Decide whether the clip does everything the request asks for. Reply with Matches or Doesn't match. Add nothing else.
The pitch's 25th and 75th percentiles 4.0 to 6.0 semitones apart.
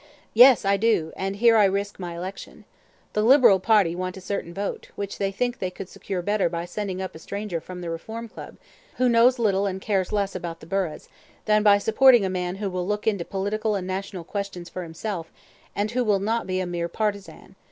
Doesn't match